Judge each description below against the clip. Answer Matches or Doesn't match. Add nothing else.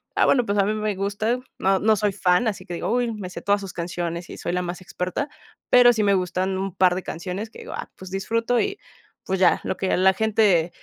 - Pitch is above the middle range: Matches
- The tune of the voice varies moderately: Matches